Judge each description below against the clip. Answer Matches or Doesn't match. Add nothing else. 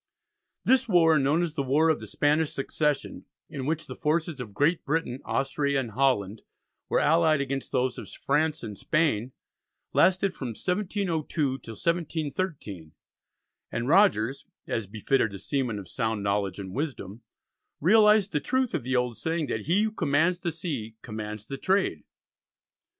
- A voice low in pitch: Doesn't match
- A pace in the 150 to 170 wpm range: Matches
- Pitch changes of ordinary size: Doesn't match